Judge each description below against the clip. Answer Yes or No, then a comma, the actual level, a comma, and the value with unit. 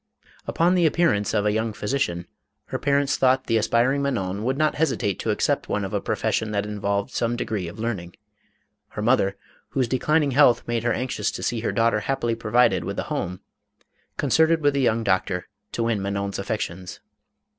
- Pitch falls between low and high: No, low, 115 Hz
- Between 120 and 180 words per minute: No, average, 190 wpm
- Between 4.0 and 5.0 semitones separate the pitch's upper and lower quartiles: Yes, average, 4.7 semitones